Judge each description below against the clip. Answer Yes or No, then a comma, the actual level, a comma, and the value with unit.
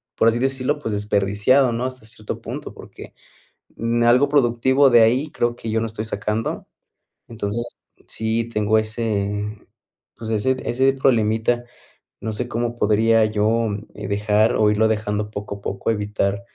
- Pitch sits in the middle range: No, low, 110 Hz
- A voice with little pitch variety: Yes, narrow, 2.2 semitones